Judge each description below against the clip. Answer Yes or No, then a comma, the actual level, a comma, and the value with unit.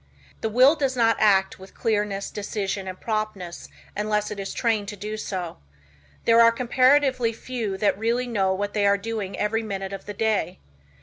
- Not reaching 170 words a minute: No, average, 180 wpm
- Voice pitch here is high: Yes, high, 210 Hz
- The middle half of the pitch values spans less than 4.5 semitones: Yes, average, 2.7 semitones